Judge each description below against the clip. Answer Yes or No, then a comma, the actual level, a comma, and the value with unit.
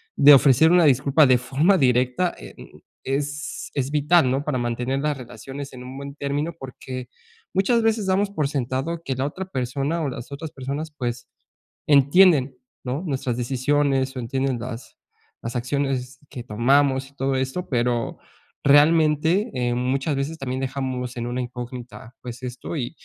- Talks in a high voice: No, low, 135 Hz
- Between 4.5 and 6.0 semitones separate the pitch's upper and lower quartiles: No, average, 2.8 semitones